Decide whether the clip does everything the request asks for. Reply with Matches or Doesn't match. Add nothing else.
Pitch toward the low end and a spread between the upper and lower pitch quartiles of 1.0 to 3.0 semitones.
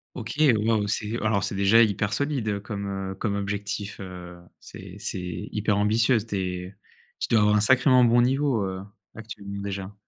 Matches